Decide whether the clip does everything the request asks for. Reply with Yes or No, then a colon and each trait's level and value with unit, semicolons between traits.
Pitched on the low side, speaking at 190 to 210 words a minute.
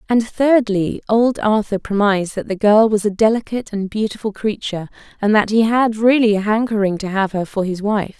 No: high, 210 Hz; average, 200 wpm